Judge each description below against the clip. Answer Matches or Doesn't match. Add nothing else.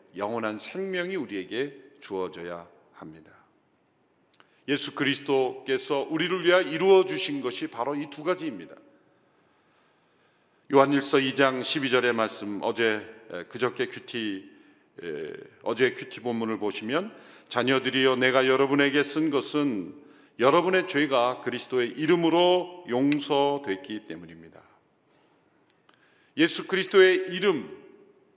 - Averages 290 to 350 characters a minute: Doesn't match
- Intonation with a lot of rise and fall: Matches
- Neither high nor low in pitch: Matches